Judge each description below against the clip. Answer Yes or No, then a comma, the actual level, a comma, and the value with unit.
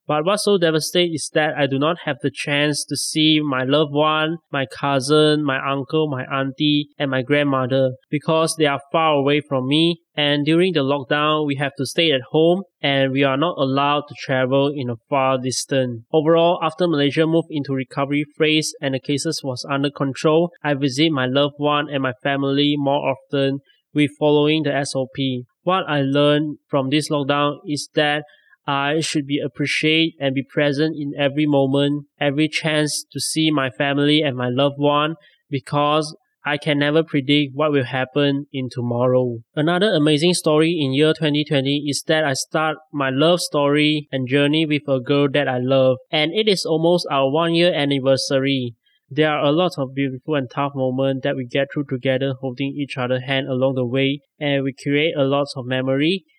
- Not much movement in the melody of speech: Yes, narrow, 2.1 semitones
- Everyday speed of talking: Yes, average, 185 wpm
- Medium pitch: Yes, medium, 145 Hz